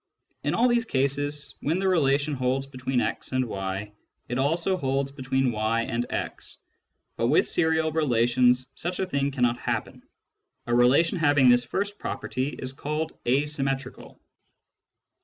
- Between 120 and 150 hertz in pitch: Yes, low, 135 Hz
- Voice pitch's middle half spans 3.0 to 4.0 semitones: Yes, average, 3.6 semitones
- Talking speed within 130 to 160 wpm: Yes, average, 145 wpm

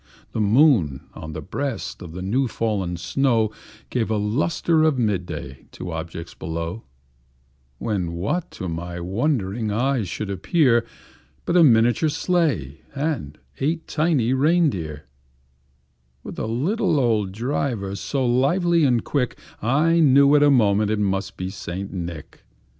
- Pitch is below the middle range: Yes, low, 115 Hz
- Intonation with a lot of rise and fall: Yes, wide, 7.3 semitones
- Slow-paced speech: No, average, 145 wpm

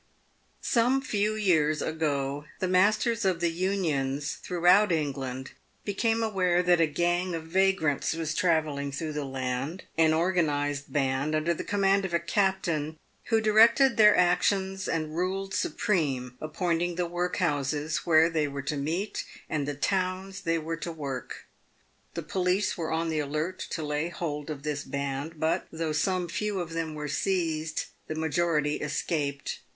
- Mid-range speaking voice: Yes, medium, 165 Hz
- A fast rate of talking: No, average, 160 wpm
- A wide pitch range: No, average, 3.8 semitones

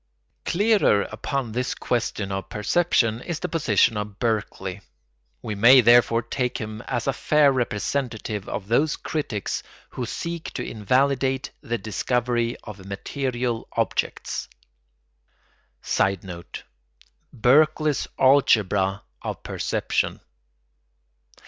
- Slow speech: Yes, slow, 105 wpm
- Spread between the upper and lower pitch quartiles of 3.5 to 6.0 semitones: Yes, average, 4.4 semitones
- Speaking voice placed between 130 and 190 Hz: No, low, 120 Hz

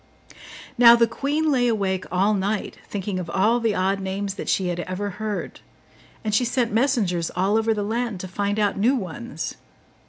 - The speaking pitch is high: Yes, high, 205 Hz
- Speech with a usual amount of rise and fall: Yes, average, 3.5 semitones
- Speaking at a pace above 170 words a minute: Yes, average, 185 wpm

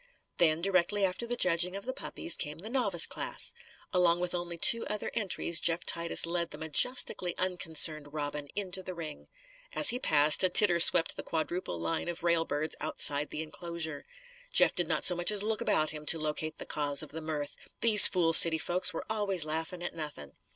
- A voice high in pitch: No, medium, 170 Hz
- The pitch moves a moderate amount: Yes, average, 3.0 semitones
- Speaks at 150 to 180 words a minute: No, average, 195 wpm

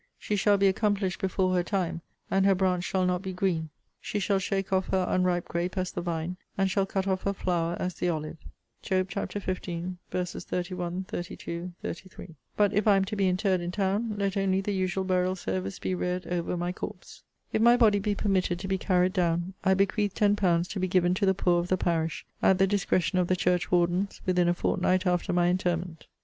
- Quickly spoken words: Yes, fast, 215 wpm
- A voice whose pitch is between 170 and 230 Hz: Yes, medium, 185 Hz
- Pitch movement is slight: Yes, narrow, 1.6 semitones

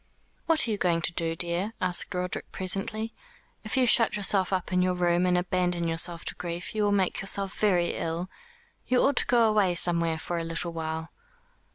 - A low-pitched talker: No, medium, 180 Hz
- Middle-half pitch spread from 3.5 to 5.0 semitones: No, average, 3.0 semitones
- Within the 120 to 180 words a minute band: No, average, 200 wpm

